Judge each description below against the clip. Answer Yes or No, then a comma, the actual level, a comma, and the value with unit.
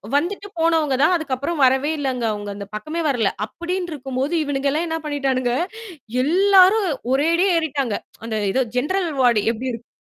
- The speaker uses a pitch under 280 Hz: No, very high, 285 Hz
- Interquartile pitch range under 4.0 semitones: No, average, 4.7 semitones